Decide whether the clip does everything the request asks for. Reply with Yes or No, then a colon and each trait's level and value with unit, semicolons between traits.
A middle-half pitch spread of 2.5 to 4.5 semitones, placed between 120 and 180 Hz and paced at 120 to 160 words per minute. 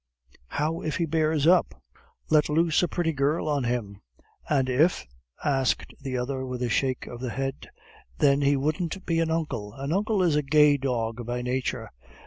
No: average, 3.9 semitones; medium, 140 Hz; average, 185 wpm